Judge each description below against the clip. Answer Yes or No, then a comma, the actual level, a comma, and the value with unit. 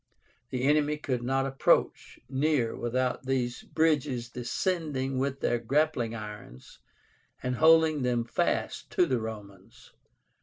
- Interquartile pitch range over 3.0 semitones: Yes, average, 3.8 semitones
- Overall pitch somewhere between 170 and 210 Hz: No, low, 130 Hz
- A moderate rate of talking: No, slow, 120 wpm